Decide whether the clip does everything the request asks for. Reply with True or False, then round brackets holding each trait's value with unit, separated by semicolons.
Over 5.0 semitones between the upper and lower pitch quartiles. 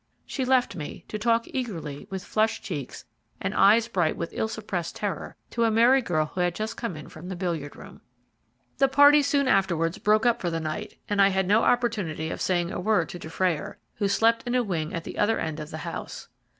True (5.5 semitones)